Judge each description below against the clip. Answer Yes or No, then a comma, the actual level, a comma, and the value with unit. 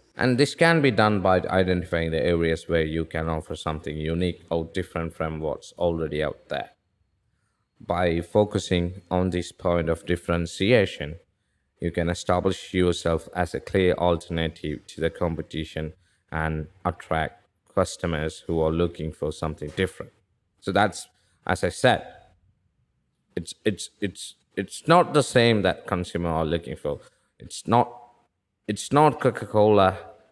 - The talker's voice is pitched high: No, very low, 85 Hz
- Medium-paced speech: No, fast, 140 wpm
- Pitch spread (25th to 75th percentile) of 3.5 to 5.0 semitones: No, average, 2.8 semitones